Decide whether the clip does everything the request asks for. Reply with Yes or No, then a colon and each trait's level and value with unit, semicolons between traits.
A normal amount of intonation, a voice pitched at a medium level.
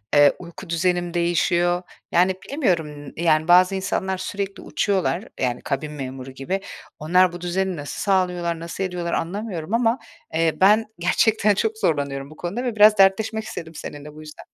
Yes: average, 3.6 semitones; medium, 175 Hz